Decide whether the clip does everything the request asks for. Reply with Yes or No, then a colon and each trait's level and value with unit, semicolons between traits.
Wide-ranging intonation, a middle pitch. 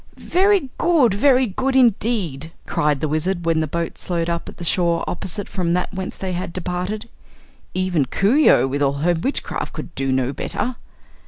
Yes: wide, 5.8 semitones; medium, 180 Hz